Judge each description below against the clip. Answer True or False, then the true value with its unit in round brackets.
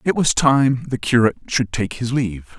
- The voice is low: True (120 Hz)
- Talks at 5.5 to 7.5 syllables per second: False (5.3 syllables/s)